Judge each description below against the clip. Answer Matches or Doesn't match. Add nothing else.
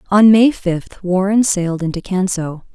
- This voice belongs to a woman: Matches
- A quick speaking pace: Doesn't match